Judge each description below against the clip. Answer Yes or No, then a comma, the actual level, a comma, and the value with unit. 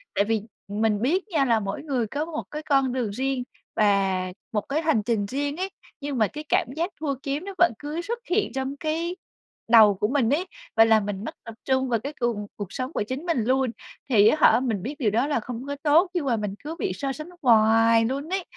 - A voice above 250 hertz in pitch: Yes, very high, 260 Hz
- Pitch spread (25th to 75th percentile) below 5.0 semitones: No, average, 5.3 semitones